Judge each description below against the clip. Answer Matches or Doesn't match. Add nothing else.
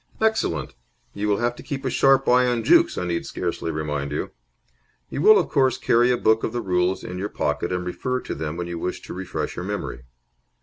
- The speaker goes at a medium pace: Doesn't match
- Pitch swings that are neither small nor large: Doesn't match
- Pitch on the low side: Matches